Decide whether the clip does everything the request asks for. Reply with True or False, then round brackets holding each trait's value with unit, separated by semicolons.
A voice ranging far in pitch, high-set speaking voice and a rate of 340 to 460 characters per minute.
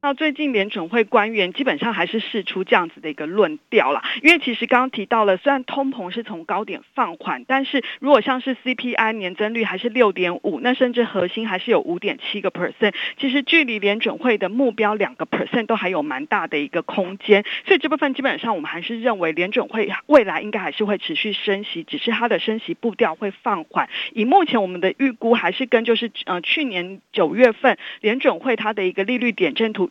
False (4.9 semitones; 230 Hz; 355 characters per minute)